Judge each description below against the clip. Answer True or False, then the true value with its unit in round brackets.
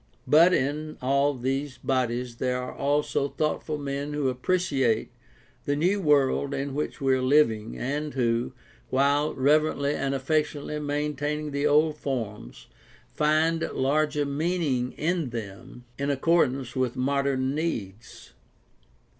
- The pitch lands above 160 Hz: False (140 Hz)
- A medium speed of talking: False (125 wpm)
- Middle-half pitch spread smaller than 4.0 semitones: True (2.6 semitones)